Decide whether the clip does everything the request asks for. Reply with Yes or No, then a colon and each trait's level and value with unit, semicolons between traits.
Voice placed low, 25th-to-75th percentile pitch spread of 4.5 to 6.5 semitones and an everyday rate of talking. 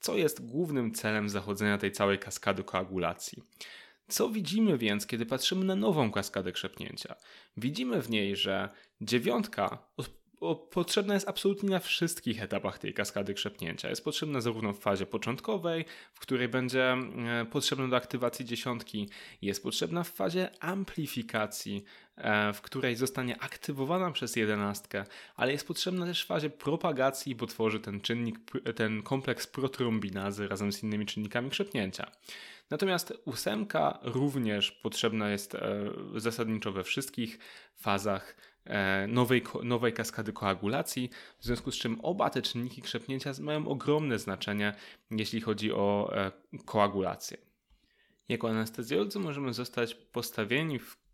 Yes: low, 120 Hz; average, 5.2 semitones; average, 130 wpm